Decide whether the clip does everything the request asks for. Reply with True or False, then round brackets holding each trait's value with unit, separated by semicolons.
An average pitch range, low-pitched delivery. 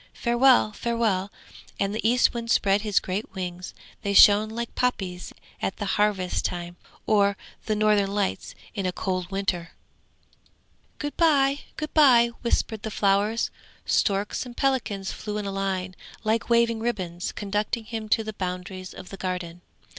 False (3.4 semitones; 205 Hz)